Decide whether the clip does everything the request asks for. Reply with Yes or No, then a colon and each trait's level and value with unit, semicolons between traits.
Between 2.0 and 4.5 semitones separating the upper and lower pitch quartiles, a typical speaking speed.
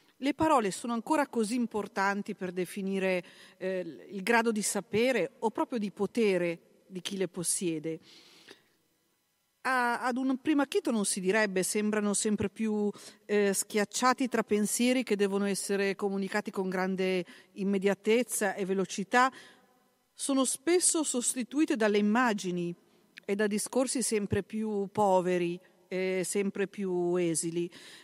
Yes: average, 4.0 semitones; average, 130 wpm